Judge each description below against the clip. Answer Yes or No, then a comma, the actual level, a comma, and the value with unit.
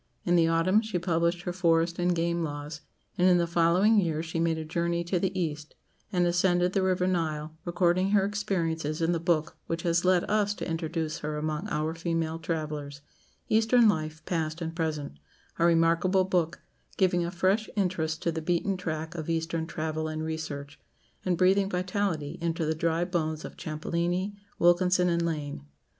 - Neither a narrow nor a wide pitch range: No, narrow, 2.1 semitones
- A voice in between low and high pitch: Yes, medium, 170 Hz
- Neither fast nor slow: Yes, average, 180 wpm